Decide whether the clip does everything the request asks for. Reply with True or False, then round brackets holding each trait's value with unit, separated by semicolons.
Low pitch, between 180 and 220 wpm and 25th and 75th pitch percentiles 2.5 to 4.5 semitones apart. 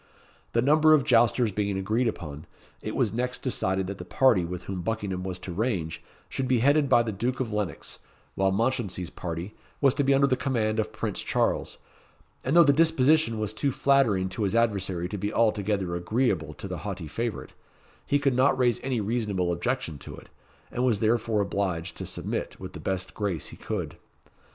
False (110 Hz; 195 wpm; 5.3 semitones)